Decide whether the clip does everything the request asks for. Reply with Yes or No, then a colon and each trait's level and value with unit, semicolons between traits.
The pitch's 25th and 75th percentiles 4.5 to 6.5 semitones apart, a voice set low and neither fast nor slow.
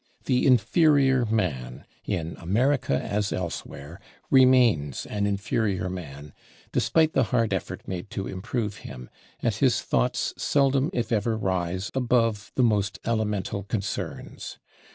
No: average, 5.1 semitones; low, 105 Hz; slow, 125 wpm